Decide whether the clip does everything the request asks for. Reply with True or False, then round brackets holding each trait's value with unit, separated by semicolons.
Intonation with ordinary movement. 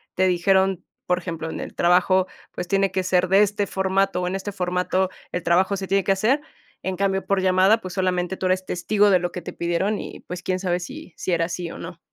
False (1.4 semitones)